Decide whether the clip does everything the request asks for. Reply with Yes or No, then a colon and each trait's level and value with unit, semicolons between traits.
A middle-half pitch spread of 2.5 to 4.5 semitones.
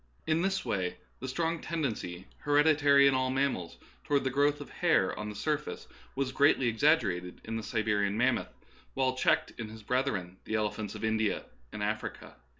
No: average, 5.2 semitones